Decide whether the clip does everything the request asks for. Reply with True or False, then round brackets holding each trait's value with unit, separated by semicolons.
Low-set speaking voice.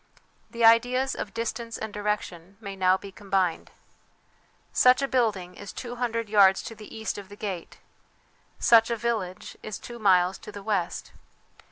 False (210 Hz)